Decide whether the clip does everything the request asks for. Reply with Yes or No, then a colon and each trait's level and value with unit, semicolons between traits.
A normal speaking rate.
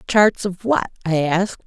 Yes: average, 180 wpm